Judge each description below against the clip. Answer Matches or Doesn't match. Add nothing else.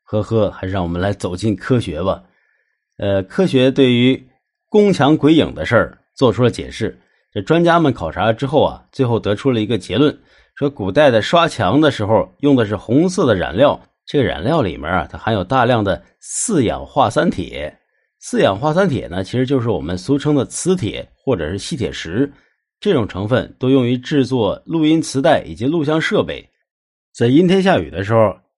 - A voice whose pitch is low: Matches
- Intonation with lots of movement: Matches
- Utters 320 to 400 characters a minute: Doesn't match